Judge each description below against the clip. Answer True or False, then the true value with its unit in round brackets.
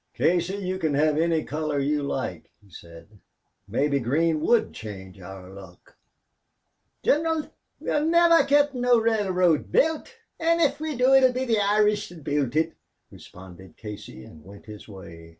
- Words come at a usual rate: True (155 wpm)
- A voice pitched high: False (160 Hz)